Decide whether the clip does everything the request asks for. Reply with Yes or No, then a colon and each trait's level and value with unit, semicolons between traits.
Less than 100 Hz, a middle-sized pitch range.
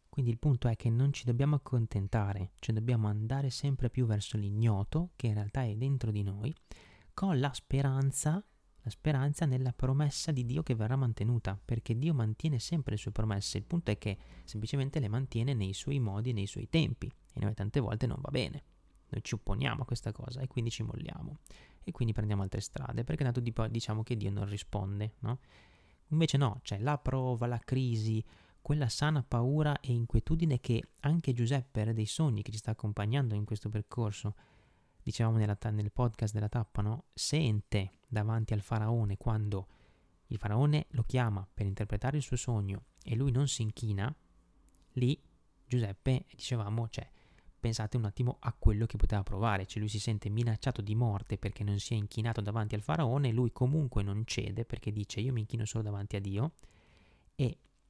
No: low, 115 Hz; average, 3.9 semitones